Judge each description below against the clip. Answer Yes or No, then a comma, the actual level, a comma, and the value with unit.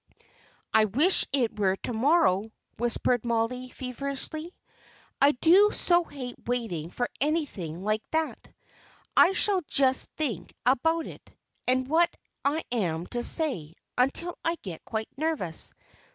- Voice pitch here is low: No, very high, 255 Hz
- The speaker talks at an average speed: No, slow, 130 wpm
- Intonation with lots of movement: Yes, wide, 6.4 semitones